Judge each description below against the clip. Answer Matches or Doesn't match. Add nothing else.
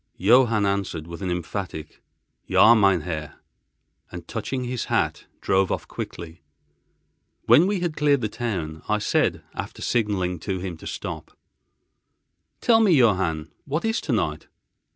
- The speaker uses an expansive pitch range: Matches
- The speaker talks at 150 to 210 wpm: Doesn't match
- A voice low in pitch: Matches